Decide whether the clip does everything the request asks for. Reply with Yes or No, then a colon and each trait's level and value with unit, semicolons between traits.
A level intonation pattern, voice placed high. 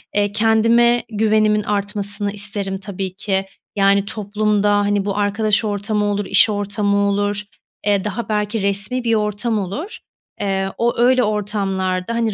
Yes: narrow, 1.3 semitones; high, 205 Hz